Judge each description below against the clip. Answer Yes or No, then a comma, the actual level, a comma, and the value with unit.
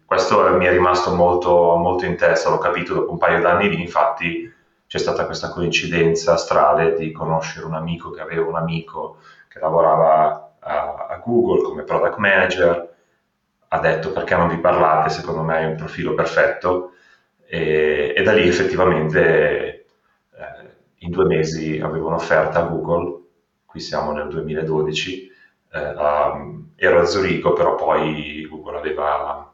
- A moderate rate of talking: Yes, average, 150 wpm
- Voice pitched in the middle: No, very low, 85 Hz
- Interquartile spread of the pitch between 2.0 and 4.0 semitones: Yes, narrow, 2.4 semitones